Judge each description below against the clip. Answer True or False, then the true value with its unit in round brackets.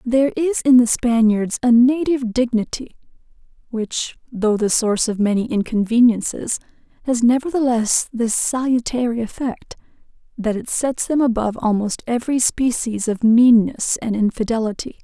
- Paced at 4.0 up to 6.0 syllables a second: True (4.9 syllables/s)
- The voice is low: False (235 Hz)